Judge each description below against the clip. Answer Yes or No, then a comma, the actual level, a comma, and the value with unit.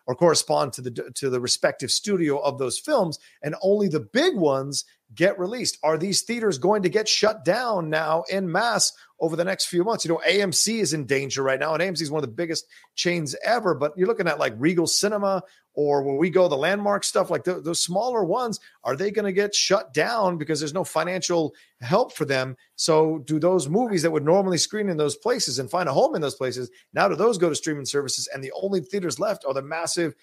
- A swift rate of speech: Yes, fast, 230 wpm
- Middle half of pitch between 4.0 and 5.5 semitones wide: Yes, average, 4.5 semitones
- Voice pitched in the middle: Yes, medium, 170 Hz